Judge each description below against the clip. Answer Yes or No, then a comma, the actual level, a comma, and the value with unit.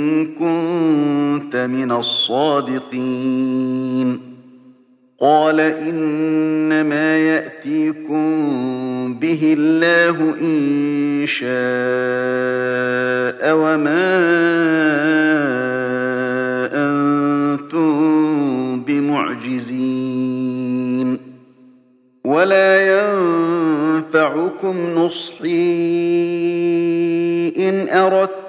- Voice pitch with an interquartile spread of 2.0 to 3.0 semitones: No, average, 4.5 semitones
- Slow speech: Yes, slow, 40 wpm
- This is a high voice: No, medium, 150 Hz